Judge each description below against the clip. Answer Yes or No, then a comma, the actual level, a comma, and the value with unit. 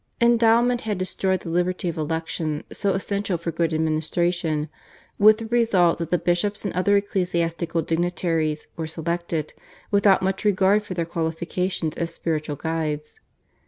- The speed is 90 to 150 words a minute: Yes, average, 145 wpm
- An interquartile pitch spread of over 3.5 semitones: No, average, 3.2 semitones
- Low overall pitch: No, medium, 175 Hz